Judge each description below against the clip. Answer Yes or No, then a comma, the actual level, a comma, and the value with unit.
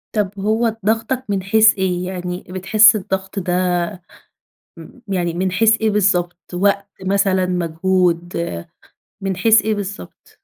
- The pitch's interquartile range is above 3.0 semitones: No, average, 2.7 semitones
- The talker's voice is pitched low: No, high, 190 Hz